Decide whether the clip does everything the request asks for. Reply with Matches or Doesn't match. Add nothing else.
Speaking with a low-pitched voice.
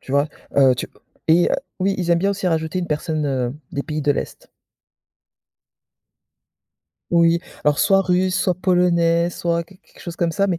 Doesn't match